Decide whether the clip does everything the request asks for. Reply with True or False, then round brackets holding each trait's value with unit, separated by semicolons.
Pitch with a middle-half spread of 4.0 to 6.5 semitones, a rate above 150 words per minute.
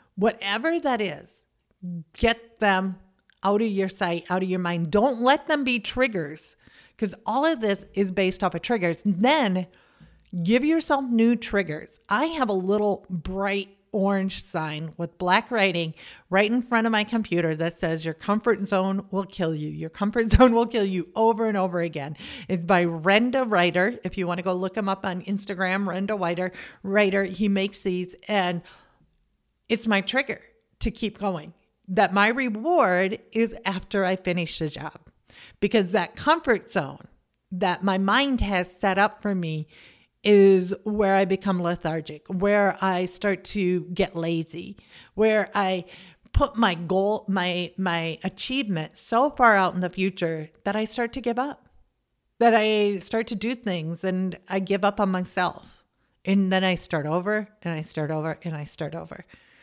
False (3.1 semitones; 170 wpm)